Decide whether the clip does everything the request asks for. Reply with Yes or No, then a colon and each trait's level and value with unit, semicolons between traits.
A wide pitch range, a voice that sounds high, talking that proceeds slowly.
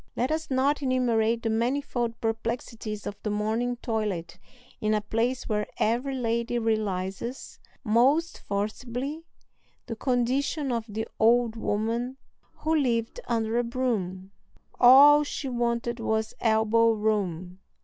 No: narrow, 2.6 semitones; high, 230 Hz; slow, 125 wpm